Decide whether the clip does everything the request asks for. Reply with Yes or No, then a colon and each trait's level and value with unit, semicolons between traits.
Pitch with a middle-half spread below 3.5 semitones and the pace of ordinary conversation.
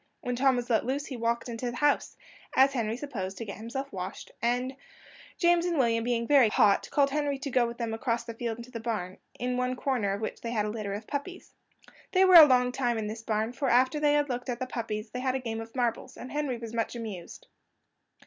No: average, 2.9 semitones; fast, 245 wpm